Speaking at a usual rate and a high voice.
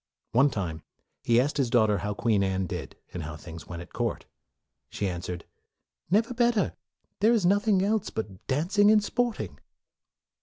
No: average, 160 wpm; low, 125 Hz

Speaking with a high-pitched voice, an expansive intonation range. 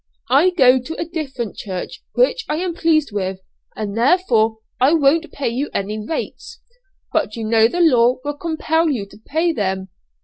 Yes: very high, 270 Hz; wide, 6.7 semitones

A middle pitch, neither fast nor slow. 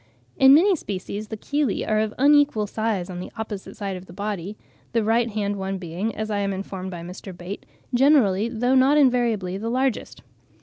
No: high, 215 Hz; average, 190 wpm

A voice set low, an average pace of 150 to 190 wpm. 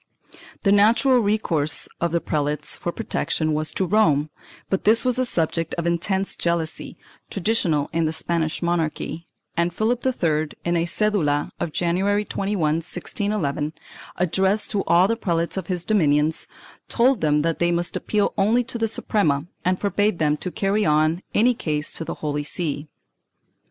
No: medium, 170 Hz; average, 160 wpm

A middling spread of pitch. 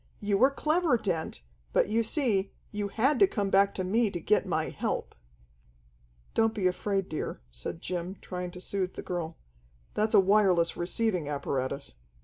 Yes: average, 3.7 semitones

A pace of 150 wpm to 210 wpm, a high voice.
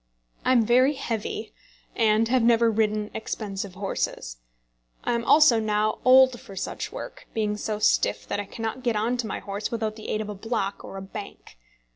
Yes: average, 190 wpm; high, 220 Hz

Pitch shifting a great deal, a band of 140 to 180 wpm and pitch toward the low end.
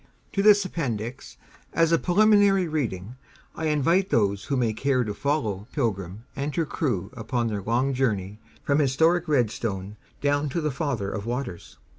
Yes: wide, 6.4 semitones; average, 160 wpm; low, 130 Hz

